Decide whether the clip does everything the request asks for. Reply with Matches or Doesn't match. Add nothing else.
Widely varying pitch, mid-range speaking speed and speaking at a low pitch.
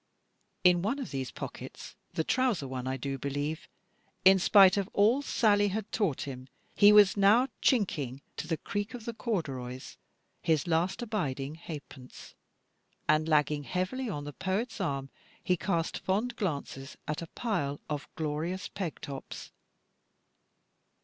Doesn't match